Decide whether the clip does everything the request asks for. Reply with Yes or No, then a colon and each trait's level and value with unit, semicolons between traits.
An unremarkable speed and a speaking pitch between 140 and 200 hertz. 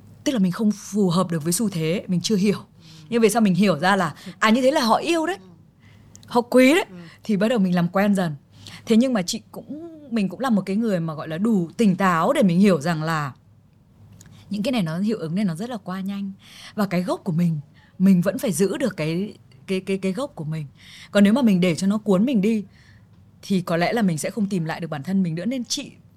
No: fast, 260 wpm; high, 195 Hz